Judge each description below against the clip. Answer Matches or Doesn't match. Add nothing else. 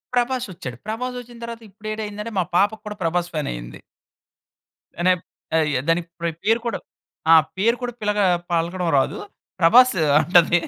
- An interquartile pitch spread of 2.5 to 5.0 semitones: Doesn't match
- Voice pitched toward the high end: Matches